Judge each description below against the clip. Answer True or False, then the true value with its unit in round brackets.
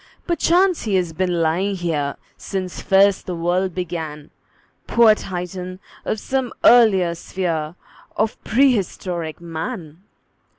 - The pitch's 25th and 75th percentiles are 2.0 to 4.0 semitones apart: True (3.7 semitones)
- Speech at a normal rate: False (115 wpm)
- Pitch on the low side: False (185 Hz)